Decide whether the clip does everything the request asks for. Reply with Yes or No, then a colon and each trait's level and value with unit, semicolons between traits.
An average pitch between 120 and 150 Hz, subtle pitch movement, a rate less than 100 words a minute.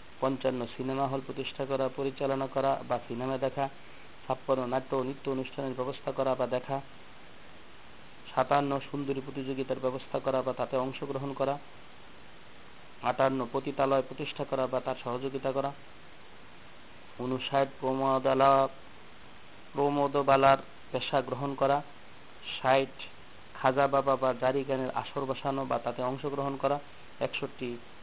No: low, 135 Hz; narrow, 1.0 semitones; average, 115 wpm